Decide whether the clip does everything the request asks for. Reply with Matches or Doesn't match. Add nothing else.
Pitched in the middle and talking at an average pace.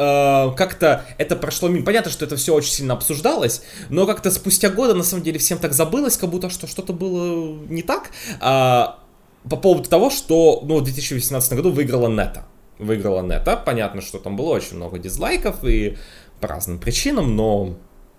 Doesn't match